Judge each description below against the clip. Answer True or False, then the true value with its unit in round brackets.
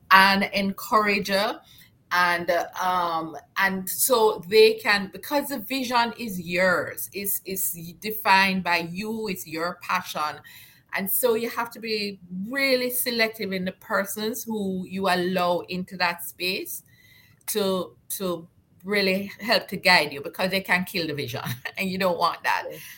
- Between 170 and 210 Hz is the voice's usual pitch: True (190 Hz)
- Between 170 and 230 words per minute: False (145 wpm)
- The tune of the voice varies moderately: True (3.4 semitones)